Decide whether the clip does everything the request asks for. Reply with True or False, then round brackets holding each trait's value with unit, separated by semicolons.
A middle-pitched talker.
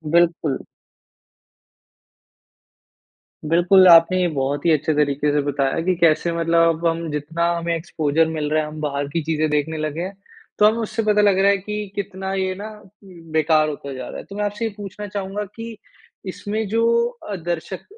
True (170 Hz)